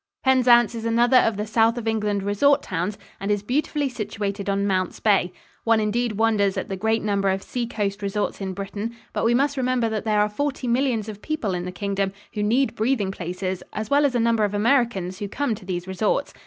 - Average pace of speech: No, fast, 215 wpm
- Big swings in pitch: No, average, 3.2 semitones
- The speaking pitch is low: No, high, 215 Hz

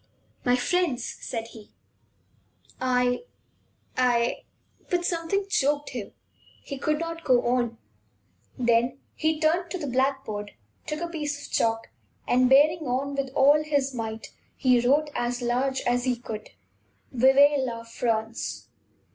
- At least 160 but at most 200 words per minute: No, average, 140 wpm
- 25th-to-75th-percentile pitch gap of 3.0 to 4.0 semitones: Yes, average, 3.6 semitones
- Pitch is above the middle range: Yes, very high, 260 Hz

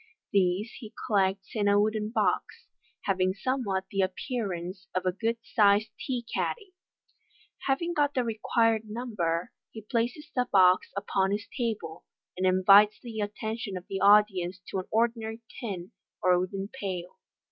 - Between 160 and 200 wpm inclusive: No, average, 145 wpm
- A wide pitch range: No, average, 3.4 semitones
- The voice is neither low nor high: No, high, 205 Hz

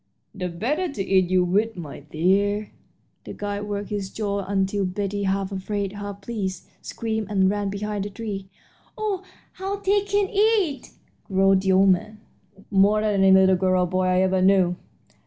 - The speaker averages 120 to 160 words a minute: No, average, 175 wpm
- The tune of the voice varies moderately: No, narrow, 2.0 semitones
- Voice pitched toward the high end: Yes, high, 200 Hz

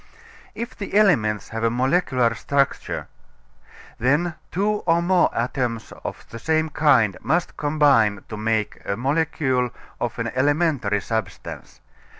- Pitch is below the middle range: Yes, low, 130 Hz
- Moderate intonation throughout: No, wide, 6.1 semitones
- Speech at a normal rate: No, slow, 130 wpm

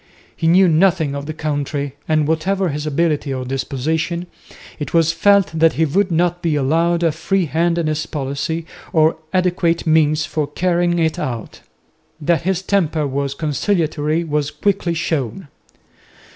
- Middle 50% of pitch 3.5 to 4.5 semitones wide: No, narrow, 2.6 semitones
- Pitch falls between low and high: Yes, medium, 160 Hz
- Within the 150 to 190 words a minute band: Yes, average, 155 wpm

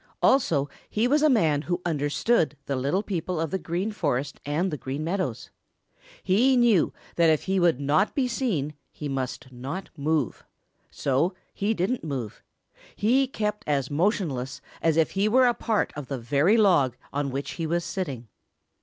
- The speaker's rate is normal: Yes, average, 170 wpm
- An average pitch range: No, wide, 6.4 semitones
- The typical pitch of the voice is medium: Yes, medium, 165 Hz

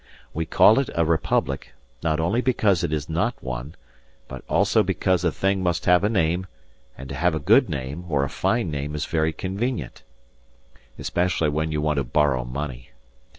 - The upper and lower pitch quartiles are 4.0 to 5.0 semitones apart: Yes, average, 4.3 semitones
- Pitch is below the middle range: Yes, very low, 80 Hz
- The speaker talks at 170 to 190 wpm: Yes, average, 185 wpm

